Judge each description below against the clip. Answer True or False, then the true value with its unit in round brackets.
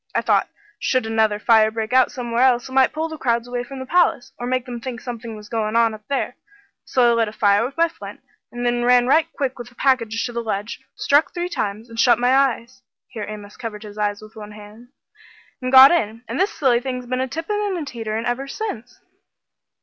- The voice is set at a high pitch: True (240 Hz)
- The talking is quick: True (235 wpm)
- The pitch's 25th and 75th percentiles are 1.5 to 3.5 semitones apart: True (2.9 semitones)